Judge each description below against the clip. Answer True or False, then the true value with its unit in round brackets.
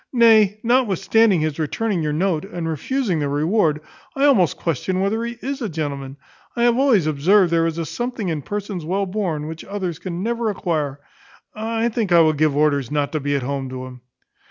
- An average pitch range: False (6.3 semitones)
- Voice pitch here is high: False (175 Hz)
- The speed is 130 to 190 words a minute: False (200 wpm)